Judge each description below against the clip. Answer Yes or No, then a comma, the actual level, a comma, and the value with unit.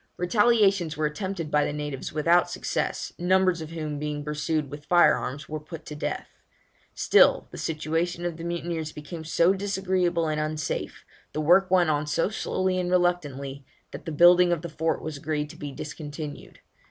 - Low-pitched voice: No, medium, 160 Hz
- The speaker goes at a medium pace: Yes, average, 175 wpm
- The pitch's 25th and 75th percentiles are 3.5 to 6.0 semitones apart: No, average, 2.9 semitones